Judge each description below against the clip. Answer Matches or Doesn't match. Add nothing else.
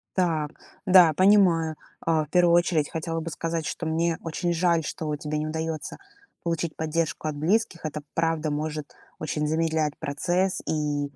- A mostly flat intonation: Matches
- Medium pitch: Matches